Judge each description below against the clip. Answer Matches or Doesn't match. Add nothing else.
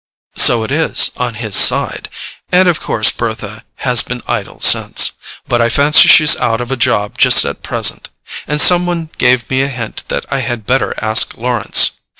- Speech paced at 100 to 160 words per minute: Doesn't match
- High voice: Doesn't match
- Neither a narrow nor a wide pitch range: Matches